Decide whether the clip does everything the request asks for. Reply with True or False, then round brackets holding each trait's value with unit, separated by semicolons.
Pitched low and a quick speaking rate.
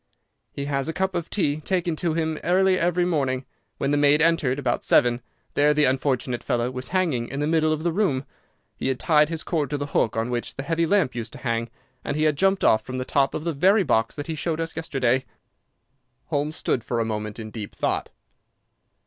False (145 Hz; 225 wpm)